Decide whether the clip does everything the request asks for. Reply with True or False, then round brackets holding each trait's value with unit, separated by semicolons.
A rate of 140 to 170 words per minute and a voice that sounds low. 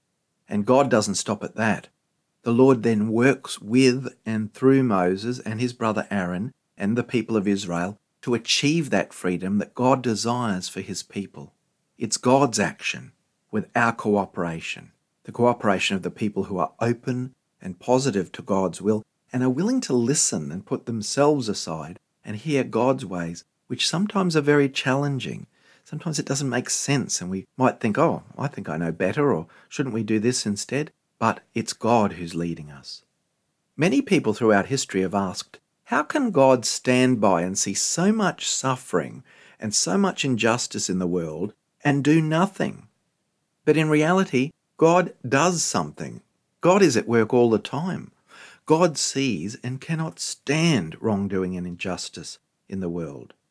True (165 wpm; 125 Hz)